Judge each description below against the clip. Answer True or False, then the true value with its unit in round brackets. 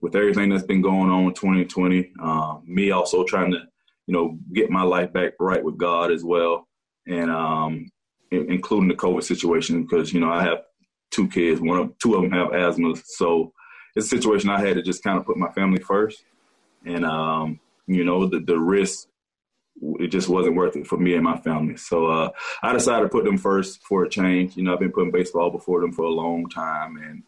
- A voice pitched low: True (90 Hz)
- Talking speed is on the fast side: True (220 wpm)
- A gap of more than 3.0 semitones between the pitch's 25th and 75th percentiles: False (2.5 semitones)